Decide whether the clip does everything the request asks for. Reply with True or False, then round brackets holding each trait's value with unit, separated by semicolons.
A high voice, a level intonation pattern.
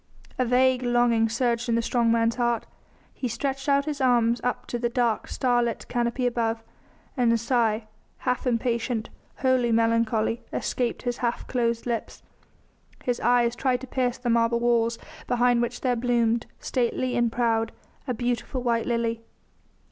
True (240 Hz; 1.3 semitones)